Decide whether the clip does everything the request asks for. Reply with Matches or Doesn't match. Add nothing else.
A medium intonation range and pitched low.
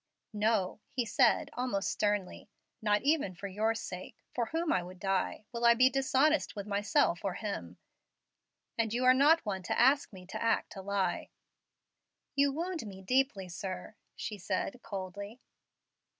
Doesn't match